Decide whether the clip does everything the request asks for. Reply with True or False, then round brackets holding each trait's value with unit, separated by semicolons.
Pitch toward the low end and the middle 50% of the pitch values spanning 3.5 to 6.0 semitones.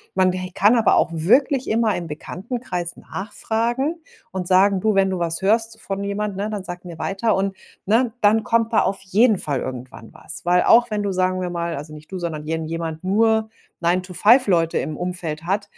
False (190 Hz; 4.1 semitones)